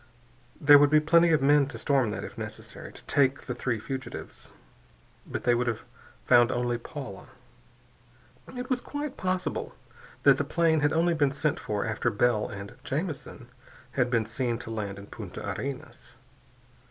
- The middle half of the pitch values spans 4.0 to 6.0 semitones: Yes, average, 4.3 semitones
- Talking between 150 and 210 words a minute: Yes, average, 165 wpm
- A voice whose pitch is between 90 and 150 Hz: Yes, low, 135 Hz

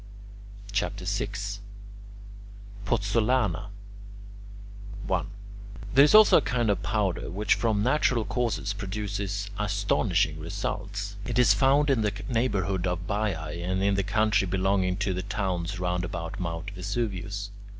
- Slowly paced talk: Yes, slow, 130 wpm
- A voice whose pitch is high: No, low, 100 Hz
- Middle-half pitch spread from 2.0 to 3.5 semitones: Yes, narrow, 2.4 semitones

